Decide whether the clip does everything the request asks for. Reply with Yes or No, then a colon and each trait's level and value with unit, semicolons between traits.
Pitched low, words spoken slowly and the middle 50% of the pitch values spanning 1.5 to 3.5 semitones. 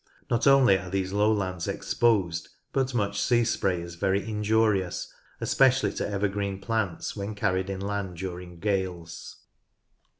Yes: low, 100 Hz; slow, 130 wpm; average, 2.7 semitones